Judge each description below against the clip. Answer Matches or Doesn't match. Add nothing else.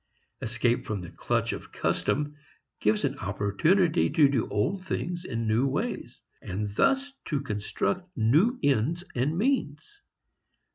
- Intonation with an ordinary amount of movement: Doesn't match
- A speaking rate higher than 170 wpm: Doesn't match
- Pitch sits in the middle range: Matches